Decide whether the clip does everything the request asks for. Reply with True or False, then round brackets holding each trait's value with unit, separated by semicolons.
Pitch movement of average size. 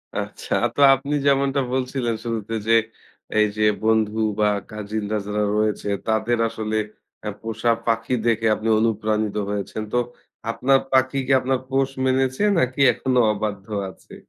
True (3.3 semitones)